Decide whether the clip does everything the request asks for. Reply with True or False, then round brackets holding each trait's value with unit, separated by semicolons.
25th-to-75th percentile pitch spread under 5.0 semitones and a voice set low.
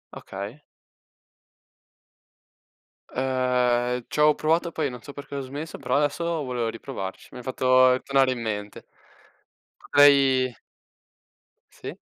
True (2.6 semitones; 130 Hz)